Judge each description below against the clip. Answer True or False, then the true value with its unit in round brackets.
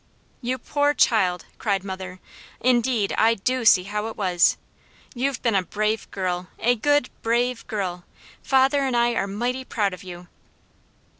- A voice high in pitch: True (220 Hz)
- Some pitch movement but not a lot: True (4.7 semitones)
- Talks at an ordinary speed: True (155 wpm)